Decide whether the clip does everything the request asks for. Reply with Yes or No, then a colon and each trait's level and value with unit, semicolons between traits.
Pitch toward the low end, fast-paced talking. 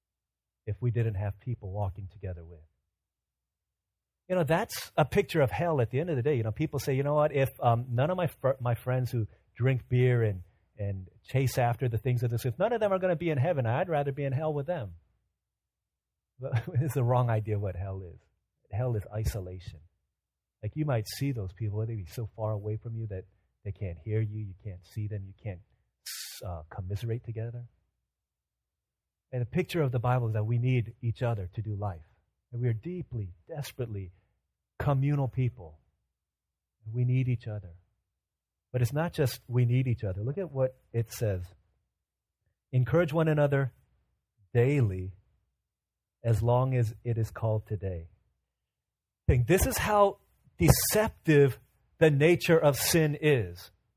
No: low, 115 Hz; average, 180 wpm